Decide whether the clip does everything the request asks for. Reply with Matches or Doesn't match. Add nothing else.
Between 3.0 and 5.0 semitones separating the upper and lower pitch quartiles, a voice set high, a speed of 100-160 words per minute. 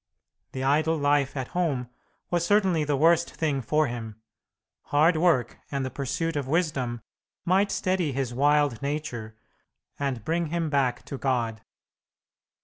Doesn't match